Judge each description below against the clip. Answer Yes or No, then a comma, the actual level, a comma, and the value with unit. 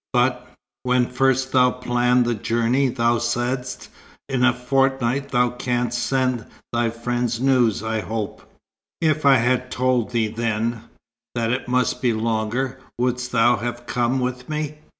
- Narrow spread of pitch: Yes, narrow, 1.5 semitones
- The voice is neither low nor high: No, low, 125 Hz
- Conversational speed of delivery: Yes, average, 150 wpm